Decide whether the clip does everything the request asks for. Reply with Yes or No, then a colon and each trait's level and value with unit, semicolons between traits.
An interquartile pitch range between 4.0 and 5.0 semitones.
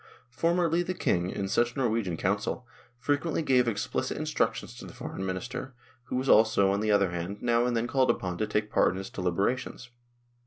Yes: average, 4.6 semitones